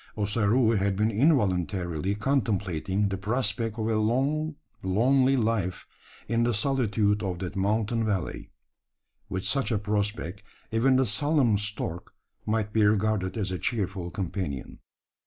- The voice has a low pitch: Yes, low, 105 Hz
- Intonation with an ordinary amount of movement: Yes, average, 3.1 semitones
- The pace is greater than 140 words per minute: No, slow, 135 wpm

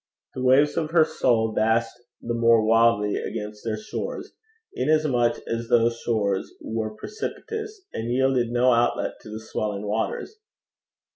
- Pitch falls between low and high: No, low, 115 Hz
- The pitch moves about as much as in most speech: Yes, average, 3.1 semitones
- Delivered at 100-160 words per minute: Yes, average, 140 wpm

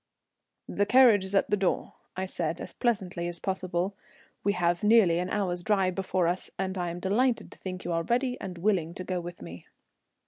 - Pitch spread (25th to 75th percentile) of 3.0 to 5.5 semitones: No, narrow, 2.6 semitones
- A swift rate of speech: Yes, fast, 210 wpm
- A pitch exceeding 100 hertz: Yes, medium, 185 Hz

